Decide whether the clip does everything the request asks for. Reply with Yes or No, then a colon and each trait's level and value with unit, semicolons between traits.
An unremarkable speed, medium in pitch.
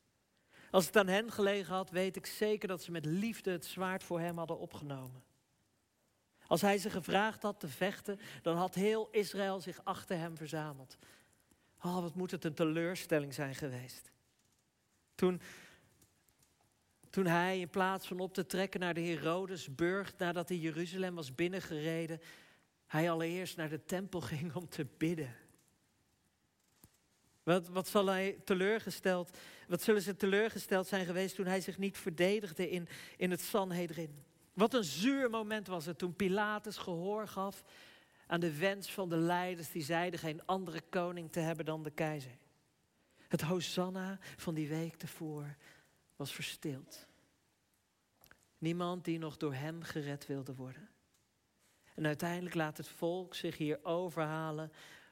Yes: average, 150 wpm; medium, 175 Hz